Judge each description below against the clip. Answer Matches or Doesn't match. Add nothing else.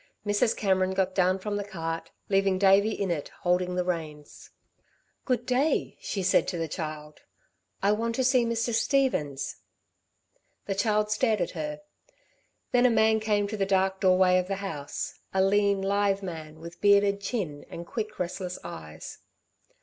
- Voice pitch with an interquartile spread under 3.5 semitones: Matches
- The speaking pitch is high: Matches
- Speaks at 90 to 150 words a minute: Doesn't match